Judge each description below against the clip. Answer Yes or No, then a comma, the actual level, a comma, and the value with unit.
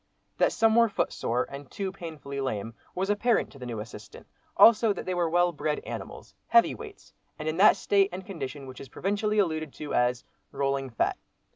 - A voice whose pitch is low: No, medium, 165 Hz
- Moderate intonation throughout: No, wide, 6.7 semitones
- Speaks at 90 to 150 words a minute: No, average, 190 wpm